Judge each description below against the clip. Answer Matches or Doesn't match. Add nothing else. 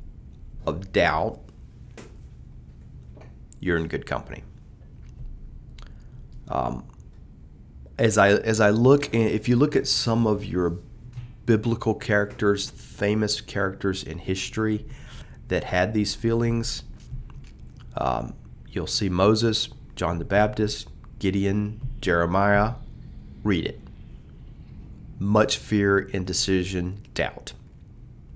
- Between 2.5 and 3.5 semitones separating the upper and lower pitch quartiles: Matches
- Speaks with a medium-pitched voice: Doesn't match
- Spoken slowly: Matches